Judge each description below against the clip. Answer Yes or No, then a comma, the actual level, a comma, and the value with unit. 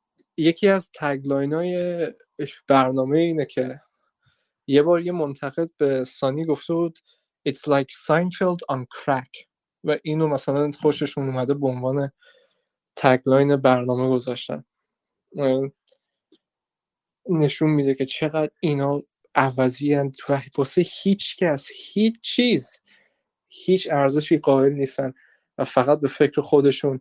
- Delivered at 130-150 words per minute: No, average, 115 wpm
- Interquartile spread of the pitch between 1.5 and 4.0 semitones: Yes, average, 3.4 semitones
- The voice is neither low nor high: Yes, medium, 145 Hz